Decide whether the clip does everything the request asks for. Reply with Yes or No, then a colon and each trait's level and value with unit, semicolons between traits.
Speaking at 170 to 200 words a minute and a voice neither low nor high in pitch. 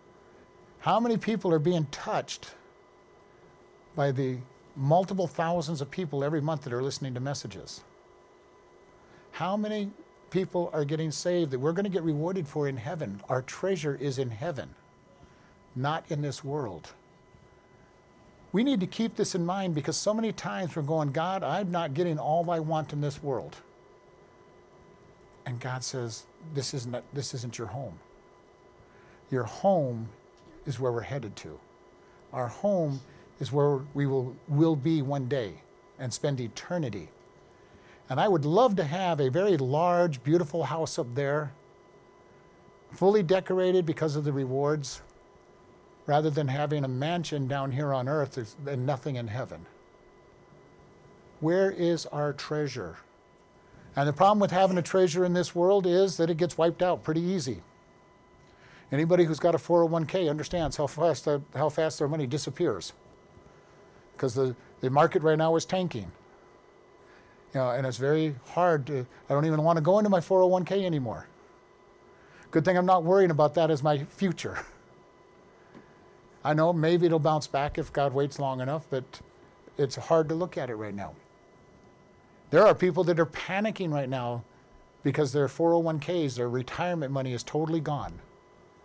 No: average, 160 wpm; medium, 155 Hz